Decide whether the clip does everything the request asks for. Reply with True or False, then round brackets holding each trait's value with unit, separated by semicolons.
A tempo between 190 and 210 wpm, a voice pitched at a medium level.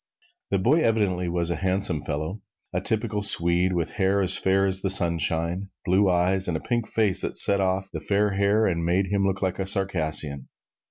False (200 wpm; 95 Hz)